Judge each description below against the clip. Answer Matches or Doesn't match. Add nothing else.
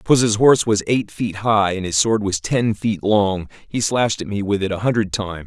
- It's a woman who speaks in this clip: Doesn't match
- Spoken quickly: Matches